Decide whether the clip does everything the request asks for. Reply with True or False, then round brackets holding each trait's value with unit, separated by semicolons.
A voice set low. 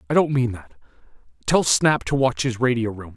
True (120 Hz)